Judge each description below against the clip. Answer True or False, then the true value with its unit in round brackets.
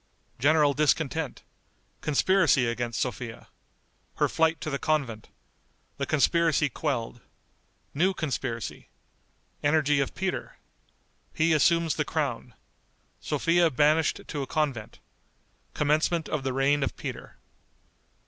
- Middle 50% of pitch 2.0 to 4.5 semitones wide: True (3.2 semitones)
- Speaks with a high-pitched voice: False (150 Hz)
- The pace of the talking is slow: True (110 wpm)